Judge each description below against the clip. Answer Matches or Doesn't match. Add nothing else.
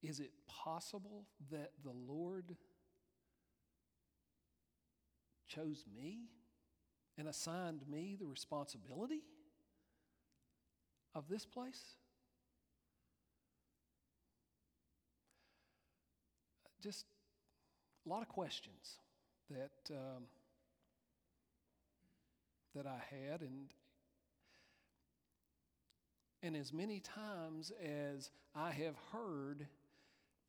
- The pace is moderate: Doesn't match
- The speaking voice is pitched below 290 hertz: Matches